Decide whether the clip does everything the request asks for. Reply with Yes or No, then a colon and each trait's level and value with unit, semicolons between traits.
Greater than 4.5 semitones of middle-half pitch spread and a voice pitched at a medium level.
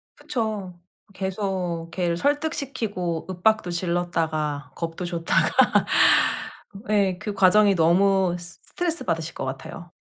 No: average, 3.4 semitones; medium, 180 Hz